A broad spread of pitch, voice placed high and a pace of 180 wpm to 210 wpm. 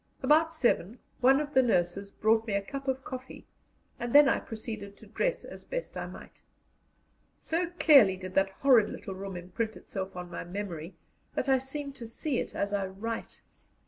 Yes: wide, 5.7 semitones; high, 225 Hz; average, 185 wpm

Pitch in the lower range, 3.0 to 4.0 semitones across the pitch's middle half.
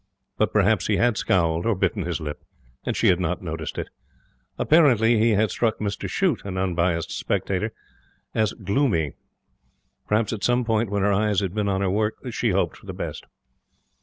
Yes: low, 100 Hz; average, 3.4 semitones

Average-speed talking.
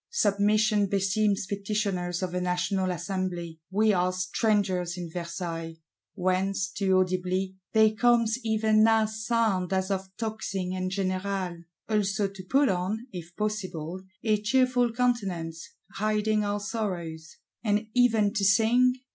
No: slow, 125 wpm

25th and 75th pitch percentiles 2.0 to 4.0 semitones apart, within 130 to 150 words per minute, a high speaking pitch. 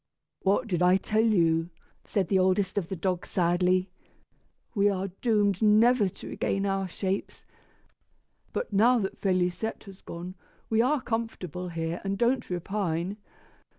Yes: average, 2.9 semitones; average, 145 wpm; high, 195 Hz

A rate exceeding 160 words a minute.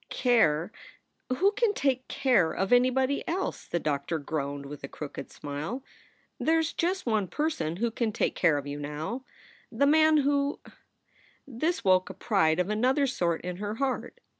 Yes: average, 170 wpm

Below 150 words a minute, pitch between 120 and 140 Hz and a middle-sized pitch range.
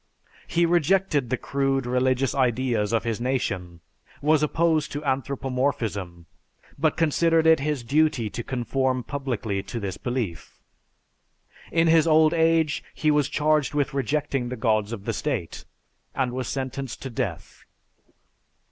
Yes: average, 140 wpm; low, 135 Hz; average, 4.3 semitones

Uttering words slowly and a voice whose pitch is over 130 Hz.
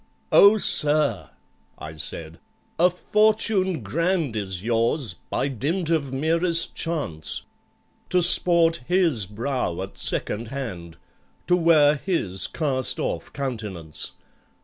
Yes: slow, 110 wpm; medium, 140 Hz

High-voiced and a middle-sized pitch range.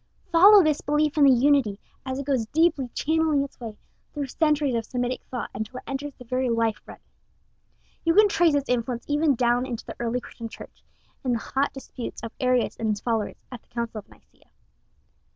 Yes: very high, 255 Hz; average, 3.8 semitones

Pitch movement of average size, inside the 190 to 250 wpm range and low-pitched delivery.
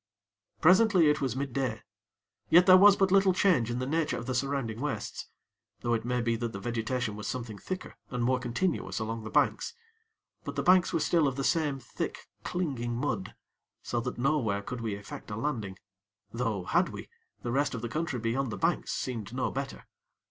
Yes: average, 4.6 semitones; average, 195 wpm; low, 125 Hz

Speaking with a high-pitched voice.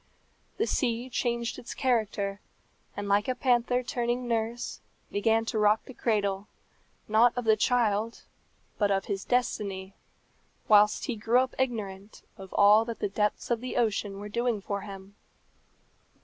Yes: high, 220 Hz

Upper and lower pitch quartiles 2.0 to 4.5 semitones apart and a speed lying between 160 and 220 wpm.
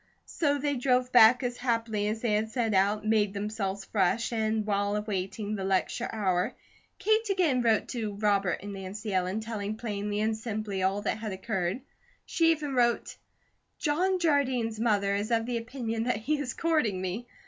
Yes: average, 3.4 semitones; average, 175 wpm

